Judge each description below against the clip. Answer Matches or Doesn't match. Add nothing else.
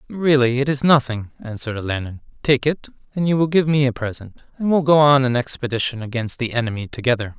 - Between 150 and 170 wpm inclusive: Doesn't match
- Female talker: Doesn't match